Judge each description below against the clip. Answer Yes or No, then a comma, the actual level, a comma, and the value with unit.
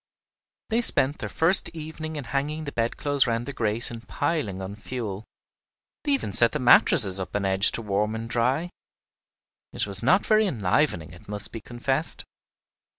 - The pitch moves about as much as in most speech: No, wide, 6.6 semitones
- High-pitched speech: No, low, 120 Hz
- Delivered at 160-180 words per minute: Yes, average, 170 wpm